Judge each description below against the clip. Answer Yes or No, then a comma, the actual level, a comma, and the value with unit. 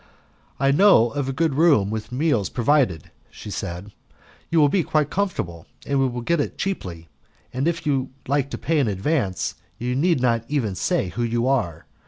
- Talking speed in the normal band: Yes, average, 185 wpm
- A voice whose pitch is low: Yes, low, 130 Hz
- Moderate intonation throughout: No, wide, 5.9 semitones